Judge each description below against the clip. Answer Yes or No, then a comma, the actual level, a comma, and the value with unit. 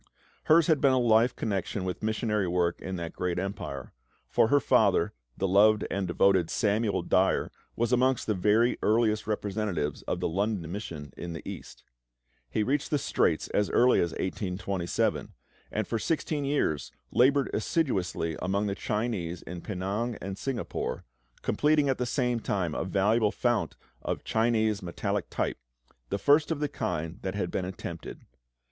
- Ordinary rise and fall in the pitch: Yes, average, 4.7 semitones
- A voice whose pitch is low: Yes, low, 105 Hz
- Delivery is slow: No, average, 165 wpm